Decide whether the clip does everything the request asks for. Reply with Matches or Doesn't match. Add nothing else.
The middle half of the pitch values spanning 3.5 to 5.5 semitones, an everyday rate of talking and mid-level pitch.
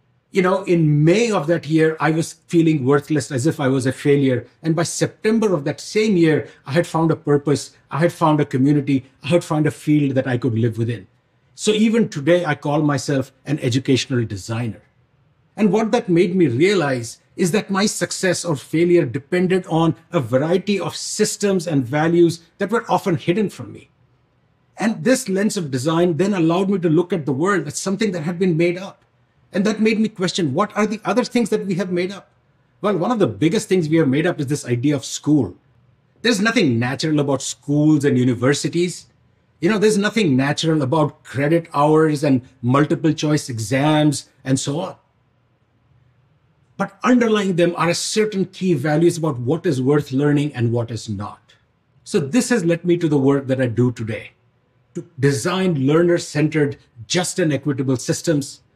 Doesn't match